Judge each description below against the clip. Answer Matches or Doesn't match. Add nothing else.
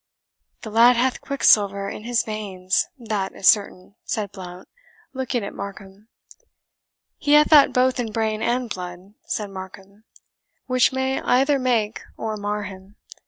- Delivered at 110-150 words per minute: Matches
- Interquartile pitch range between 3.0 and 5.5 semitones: Matches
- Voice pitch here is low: Doesn't match